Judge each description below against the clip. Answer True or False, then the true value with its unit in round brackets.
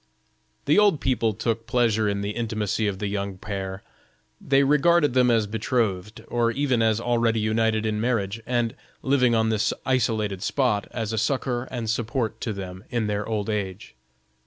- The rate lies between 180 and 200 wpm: False (170 wpm)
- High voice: False (110 Hz)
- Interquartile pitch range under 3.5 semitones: True (2.6 semitones)